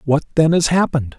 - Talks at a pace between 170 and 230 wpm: Yes, average, 200 wpm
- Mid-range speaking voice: Yes, medium, 150 Hz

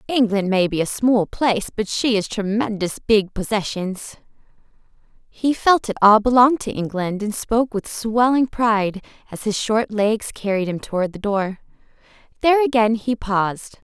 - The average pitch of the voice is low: No, high, 215 Hz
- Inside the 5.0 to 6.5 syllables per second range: No, 4.8 syllables/s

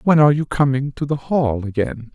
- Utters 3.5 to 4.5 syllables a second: No, 5.4 syllables/s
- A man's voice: Yes, male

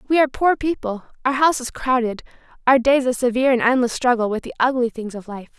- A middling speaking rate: No, fast, 225 wpm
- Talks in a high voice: Yes, very high, 250 Hz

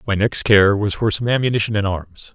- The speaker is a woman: No, male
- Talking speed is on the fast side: Yes, fast, 230 wpm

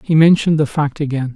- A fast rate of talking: Yes, fast, 220 wpm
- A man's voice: Yes, male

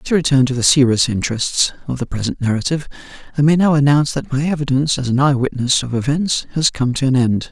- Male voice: Yes, male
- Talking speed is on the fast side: Yes, fast, 225 wpm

